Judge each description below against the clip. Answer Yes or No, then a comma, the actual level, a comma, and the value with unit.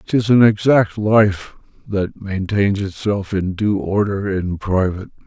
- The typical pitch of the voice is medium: No, low, 100 Hz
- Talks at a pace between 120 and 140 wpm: Yes, slow, 135 wpm